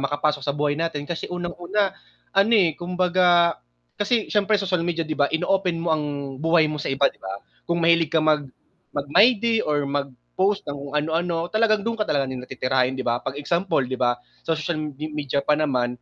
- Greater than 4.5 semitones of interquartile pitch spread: No, average, 3.9 semitones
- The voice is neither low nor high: Yes, medium, 160 Hz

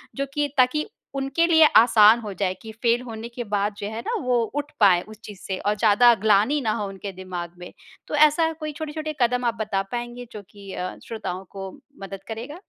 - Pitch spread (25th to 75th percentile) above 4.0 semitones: Yes, average, 4.4 semitones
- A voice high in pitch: Yes, high, 225 Hz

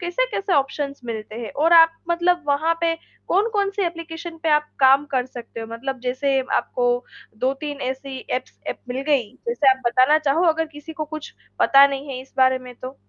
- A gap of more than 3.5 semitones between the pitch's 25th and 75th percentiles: Yes, average, 4.1 semitones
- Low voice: No, very high, 280 Hz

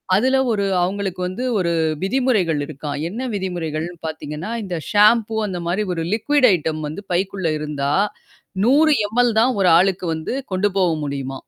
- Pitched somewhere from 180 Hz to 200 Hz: Yes, medium, 185 Hz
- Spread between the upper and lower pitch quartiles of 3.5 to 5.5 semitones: Yes, average, 5.2 semitones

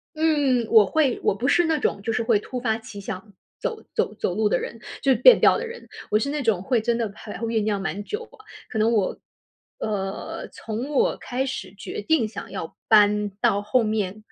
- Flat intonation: No, average, 4.2 semitones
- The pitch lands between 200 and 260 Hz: Yes, high, 225 Hz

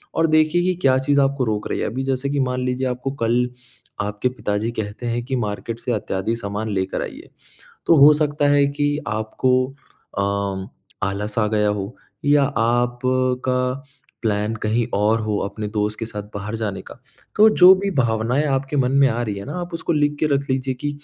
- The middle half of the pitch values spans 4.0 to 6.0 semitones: Yes, average, 4.6 semitones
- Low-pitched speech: Yes, low, 125 Hz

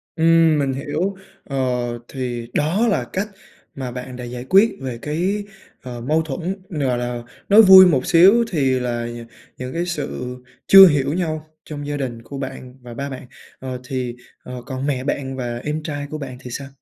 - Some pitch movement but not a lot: Yes, average, 4.4 semitones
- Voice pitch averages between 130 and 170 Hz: Yes, medium, 140 Hz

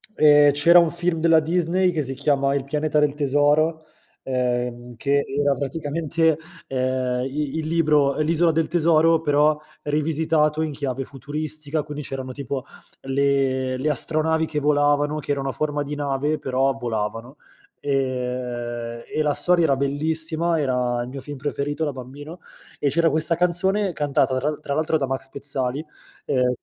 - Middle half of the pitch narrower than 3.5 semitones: Yes, average, 2.7 semitones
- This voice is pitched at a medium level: Yes, medium, 145 Hz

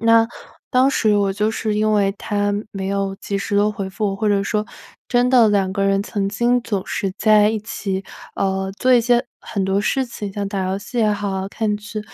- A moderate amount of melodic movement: No, narrow, 1.9 semitones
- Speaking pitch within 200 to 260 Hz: Yes, high, 205 Hz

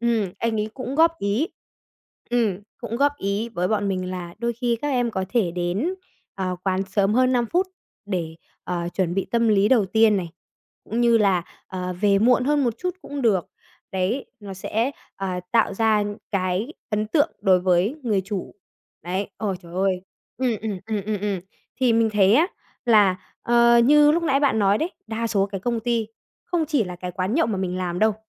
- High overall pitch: Yes, high, 215 Hz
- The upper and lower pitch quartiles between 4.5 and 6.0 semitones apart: No, average, 4.1 semitones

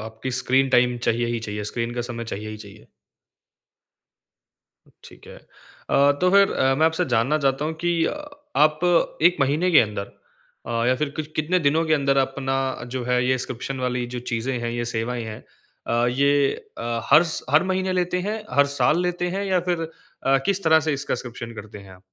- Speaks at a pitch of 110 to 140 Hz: Yes, low, 135 Hz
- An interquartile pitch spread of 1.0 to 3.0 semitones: No, average, 4.9 semitones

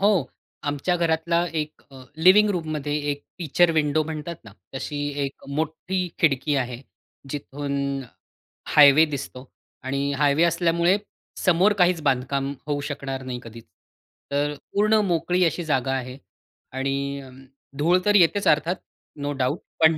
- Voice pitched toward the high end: No, medium, 150 Hz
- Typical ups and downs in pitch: Yes, average, 3.6 semitones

